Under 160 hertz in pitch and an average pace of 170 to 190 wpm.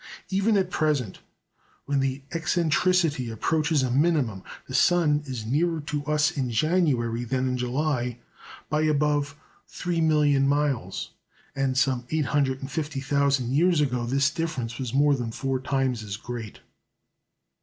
No: medium, 140 Hz; slow, 135 wpm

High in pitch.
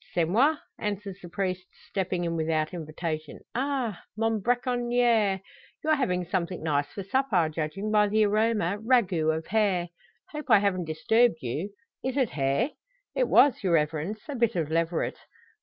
Yes: high, 195 Hz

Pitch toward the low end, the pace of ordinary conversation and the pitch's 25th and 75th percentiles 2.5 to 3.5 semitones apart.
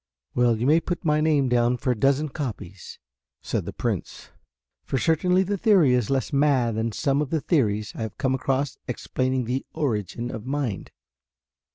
No: low, 130 Hz; average, 180 wpm; average, 4.1 semitones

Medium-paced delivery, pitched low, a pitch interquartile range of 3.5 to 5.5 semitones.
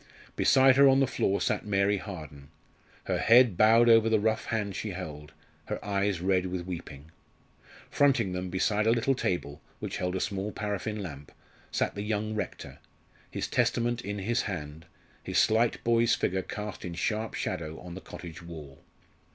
Yes: average, 170 wpm; low, 100 Hz; average, 4.0 semitones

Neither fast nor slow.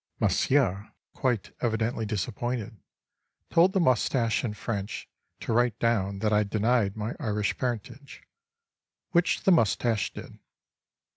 No: slow, 120 wpm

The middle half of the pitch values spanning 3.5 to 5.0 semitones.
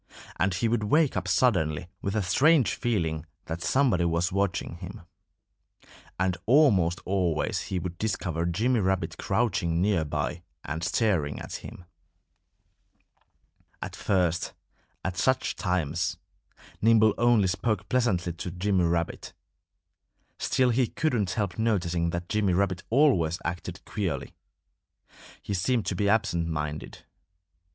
Yes: average, 4.4 semitones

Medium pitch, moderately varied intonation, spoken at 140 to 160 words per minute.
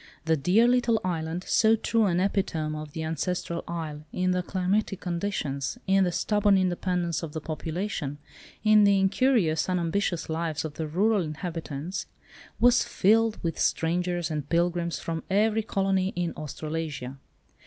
Yes: medium, 175 Hz; average, 3.6 semitones; average, 145 wpm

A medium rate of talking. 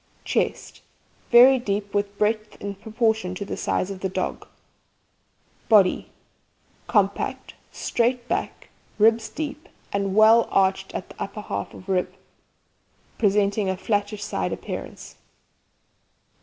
No: slow, 120 wpm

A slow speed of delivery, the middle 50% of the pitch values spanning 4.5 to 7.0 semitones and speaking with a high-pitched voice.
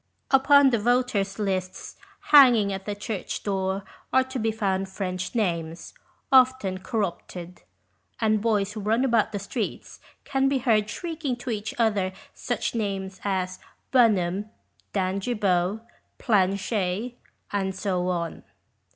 No: slow, 125 wpm; average, 3.8 semitones; high, 205 Hz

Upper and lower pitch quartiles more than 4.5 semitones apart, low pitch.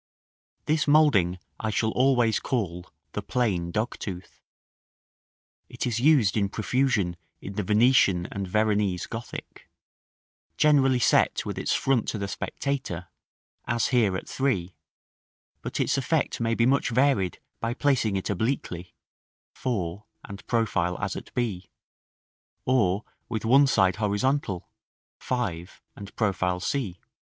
Yes: average, 5.2 semitones; low, 110 Hz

